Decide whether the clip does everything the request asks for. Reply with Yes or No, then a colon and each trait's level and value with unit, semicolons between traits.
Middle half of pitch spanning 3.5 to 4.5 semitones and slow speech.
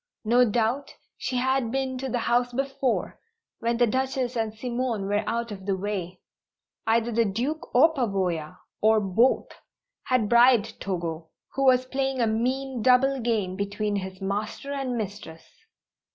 No: average, 4.0 semitones; average, 150 wpm